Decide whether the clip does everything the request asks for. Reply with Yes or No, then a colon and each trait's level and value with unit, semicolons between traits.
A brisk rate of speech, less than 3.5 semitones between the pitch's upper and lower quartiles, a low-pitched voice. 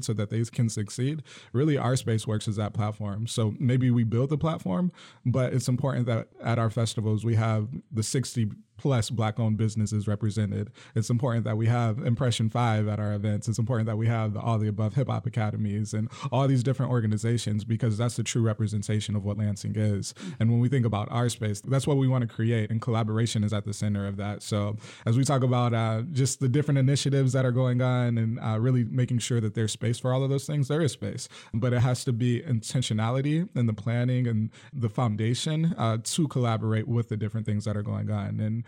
Yes: fast, 225 wpm; average, 2.7 semitones; low, 115 Hz